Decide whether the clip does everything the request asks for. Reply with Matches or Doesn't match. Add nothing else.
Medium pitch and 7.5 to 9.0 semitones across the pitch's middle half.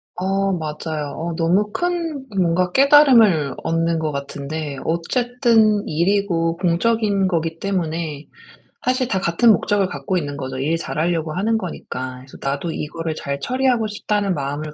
Doesn't match